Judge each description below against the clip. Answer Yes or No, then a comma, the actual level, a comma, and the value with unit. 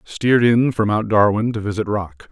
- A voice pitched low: Yes, low, 110 Hz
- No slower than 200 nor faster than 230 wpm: Yes, fast, 205 wpm